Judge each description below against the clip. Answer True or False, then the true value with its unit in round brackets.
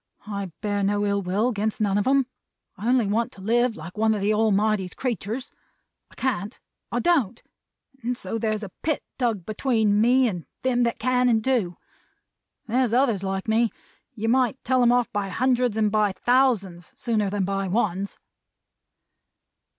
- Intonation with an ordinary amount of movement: True (3.5 semitones)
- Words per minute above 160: True (170 wpm)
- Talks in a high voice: True (220 Hz)